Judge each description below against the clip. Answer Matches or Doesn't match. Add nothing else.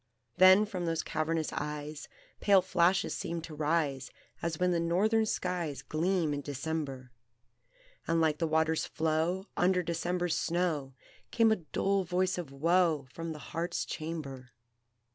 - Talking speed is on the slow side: Doesn't match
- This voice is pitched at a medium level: Matches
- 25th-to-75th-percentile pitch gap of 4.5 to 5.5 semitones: Doesn't match